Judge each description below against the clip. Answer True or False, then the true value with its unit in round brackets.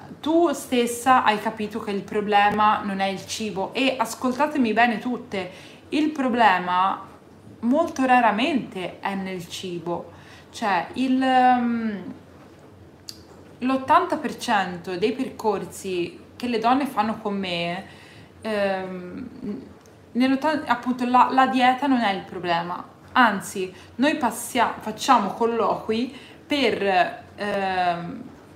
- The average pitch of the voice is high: True (225 Hz)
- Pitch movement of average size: True (4.7 semitones)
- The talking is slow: True (105 wpm)